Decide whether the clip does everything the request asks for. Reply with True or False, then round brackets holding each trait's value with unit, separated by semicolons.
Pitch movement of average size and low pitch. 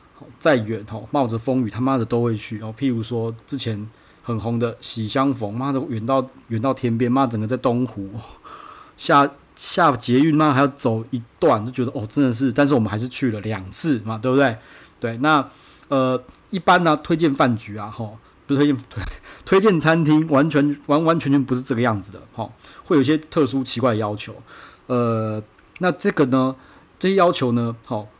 True (3.9 semitones; 125 Hz)